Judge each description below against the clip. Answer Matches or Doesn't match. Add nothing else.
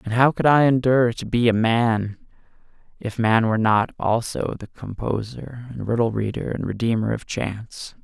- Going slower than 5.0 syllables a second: Matches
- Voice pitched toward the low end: Matches